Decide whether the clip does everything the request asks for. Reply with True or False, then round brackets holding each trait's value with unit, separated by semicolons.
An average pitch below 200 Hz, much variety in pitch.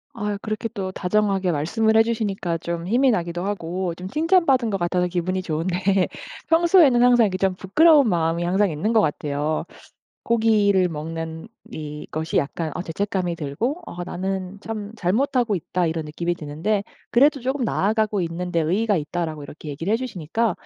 False (190 Hz; 4.9 semitones)